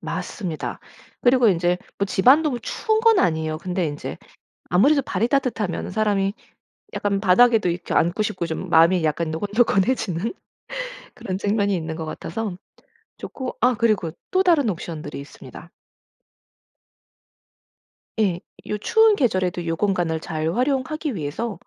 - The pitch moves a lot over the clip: Yes, wide, 6.2 semitones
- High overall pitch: Yes, high, 200 Hz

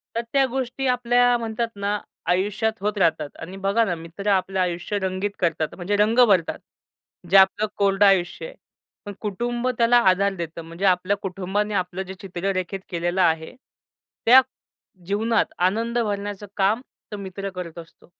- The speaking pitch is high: Yes, high, 195 Hz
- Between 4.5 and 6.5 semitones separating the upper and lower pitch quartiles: No, average, 3.2 semitones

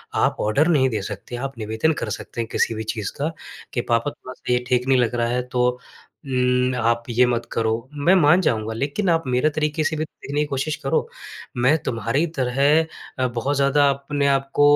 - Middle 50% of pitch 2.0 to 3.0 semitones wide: No, average, 3.5 semitones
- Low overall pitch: Yes, low, 130 Hz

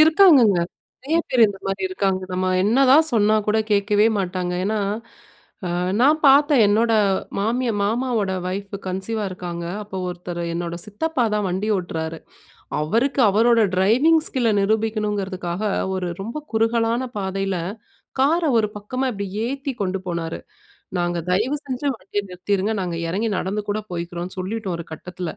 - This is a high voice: Yes, high, 205 Hz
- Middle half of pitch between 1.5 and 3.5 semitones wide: No, average, 4.0 semitones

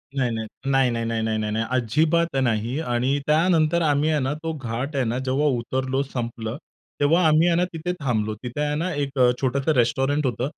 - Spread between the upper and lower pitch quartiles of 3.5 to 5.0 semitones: Yes, average, 4.3 semitones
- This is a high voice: No, low, 135 Hz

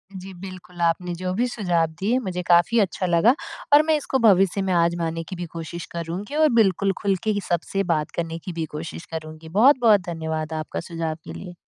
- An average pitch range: Yes, average, 3.2 semitones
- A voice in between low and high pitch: Yes, medium, 180 Hz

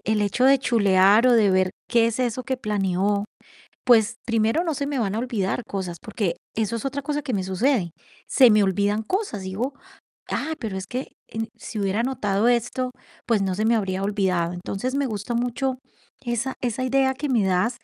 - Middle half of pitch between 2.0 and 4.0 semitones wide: No, average, 4.4 semitones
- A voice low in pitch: No, high, 225 Hz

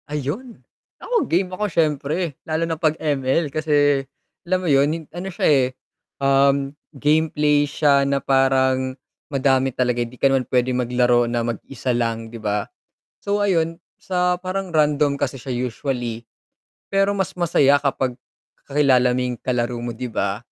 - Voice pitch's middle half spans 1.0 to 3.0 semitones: No, average, 4.2 semitones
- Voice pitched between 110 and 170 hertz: Yes, medium, 140 Hz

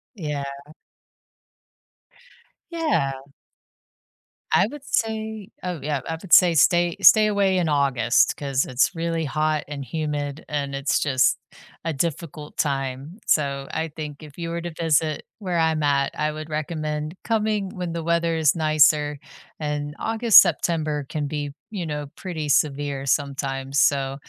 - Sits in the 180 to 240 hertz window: No, medium, 155 Hz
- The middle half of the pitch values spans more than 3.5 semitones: No, average, 3.0 semitones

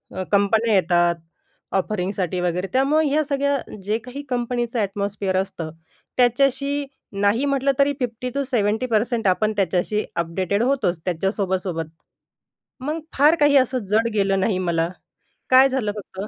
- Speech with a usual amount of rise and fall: No, wide, 5.7 semitones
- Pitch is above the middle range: Yes, high, 215 Hz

